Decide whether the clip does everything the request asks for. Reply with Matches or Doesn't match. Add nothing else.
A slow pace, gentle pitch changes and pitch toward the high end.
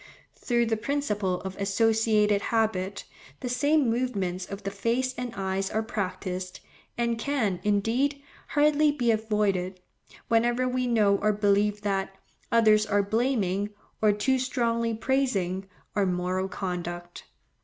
Doesn't match